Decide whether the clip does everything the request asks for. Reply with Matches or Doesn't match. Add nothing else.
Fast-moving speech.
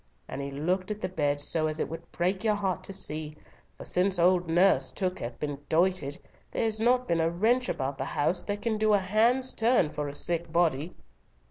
Matches